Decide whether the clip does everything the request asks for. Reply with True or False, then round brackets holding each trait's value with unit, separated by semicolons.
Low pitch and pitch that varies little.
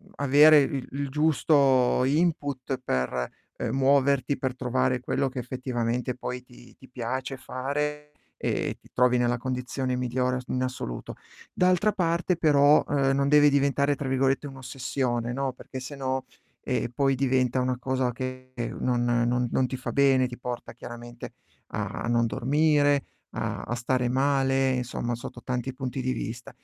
True (130 Hz; 1.9 semitones)